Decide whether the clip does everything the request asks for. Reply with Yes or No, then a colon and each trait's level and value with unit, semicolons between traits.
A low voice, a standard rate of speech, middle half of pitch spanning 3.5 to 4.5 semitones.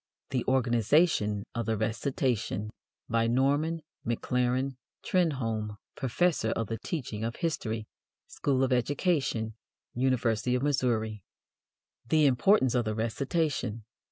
No: low, 125 Hz; slow, 110 wpm; average, 3.9 semitones